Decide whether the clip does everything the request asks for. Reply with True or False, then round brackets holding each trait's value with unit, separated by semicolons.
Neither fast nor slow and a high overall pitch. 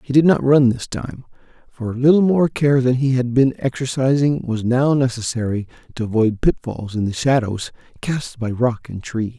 False (190 wpm; 125 Hz)